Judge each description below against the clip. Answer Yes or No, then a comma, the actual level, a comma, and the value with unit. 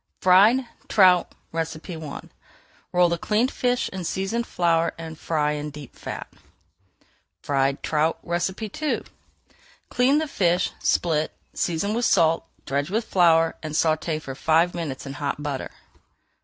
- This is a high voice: No, medium, 165 Hz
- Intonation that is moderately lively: Yes, average, 3.8 semitones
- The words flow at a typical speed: No, slow, 130 wpm